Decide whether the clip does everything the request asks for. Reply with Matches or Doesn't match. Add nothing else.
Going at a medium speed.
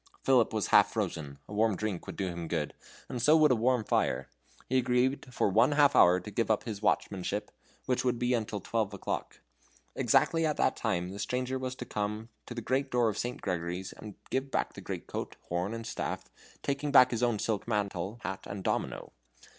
Doesn't match